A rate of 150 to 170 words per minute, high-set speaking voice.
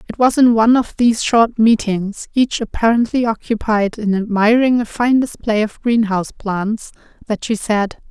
Yes: average, 165 wpm; high, 220 Hz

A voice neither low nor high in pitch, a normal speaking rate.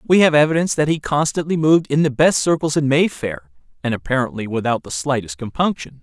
Yes: medium, 145 Hz; average, 190 wpm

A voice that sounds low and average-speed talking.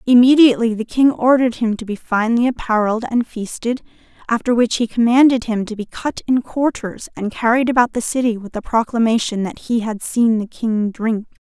No: high, 230 Hz; average, 190 wpm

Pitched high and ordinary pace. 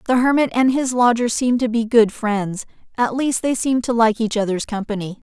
No: high, 235 Hz; fast, 215 wpm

